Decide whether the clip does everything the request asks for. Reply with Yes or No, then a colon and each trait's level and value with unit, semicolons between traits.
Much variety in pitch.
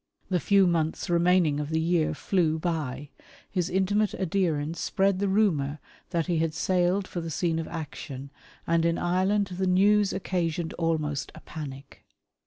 No: average, 3.0 semitones